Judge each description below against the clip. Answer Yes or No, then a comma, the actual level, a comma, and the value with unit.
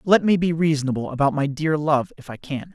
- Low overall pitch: No, medium, 150 Hz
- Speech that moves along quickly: Yes, fast, 240 wpm